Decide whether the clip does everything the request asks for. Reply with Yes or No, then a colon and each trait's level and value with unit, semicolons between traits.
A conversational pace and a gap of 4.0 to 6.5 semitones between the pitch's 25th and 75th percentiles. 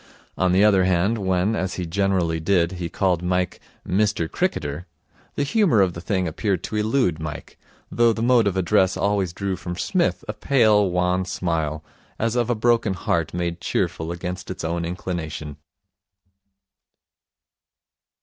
No: average, 155 wpm; average, 3.6 semitones